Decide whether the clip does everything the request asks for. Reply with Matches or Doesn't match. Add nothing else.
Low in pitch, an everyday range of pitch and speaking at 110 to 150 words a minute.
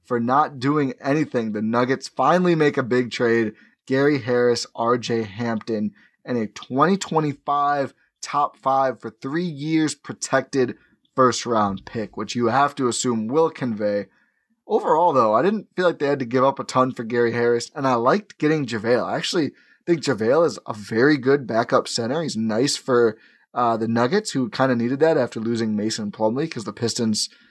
Doesn't match